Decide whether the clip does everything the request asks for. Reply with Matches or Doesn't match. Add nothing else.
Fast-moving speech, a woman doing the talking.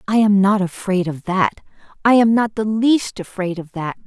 Doesn't match